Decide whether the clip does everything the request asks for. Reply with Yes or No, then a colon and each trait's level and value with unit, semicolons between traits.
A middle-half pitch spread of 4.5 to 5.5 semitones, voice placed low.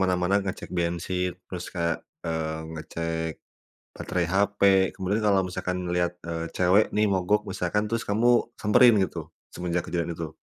No: average, 3.0 semitones; very low, 90 Hz